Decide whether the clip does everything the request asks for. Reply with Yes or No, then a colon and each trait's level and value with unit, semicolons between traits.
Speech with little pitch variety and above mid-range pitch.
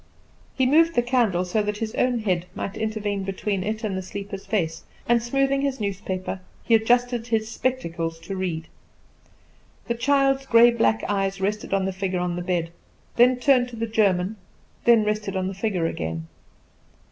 No: average, 4.1 semitones; high, 210 Hz